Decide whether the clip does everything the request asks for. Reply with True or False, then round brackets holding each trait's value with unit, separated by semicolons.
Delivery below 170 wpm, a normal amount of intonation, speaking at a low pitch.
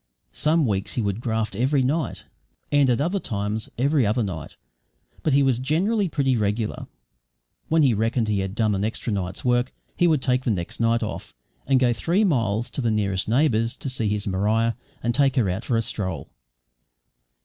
False (195 wpm; 4.4 semitones; 115 Hz)